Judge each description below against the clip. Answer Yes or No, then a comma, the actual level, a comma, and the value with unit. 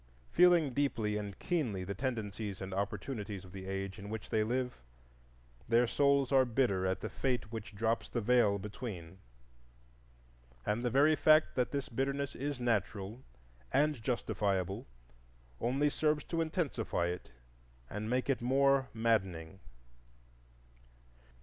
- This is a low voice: Yes, low, 115 Hz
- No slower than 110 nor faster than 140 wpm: Yes, slow, 135 wpm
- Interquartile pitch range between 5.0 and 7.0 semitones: Yes, average, 5.3 semitones